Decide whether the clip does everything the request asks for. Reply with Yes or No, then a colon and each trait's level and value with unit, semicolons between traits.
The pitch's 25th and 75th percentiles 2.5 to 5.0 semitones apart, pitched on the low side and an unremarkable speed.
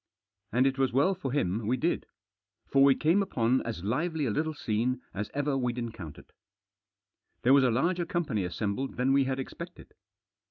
Yes: average, 4.0 semitones; low, 130 Hz; average, 175 wpm